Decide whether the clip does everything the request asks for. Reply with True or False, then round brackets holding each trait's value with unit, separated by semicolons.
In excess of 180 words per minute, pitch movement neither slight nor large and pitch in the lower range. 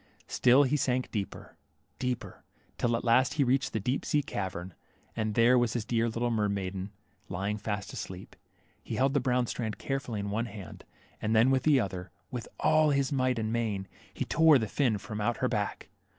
True (200 wpm; 3.7 semitones; 115 Hz)